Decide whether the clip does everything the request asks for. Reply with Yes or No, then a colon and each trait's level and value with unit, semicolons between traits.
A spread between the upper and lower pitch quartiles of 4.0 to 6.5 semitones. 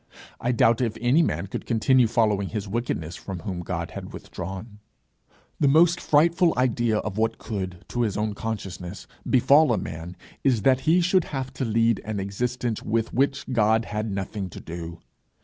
Yes: average, 4.4 semitones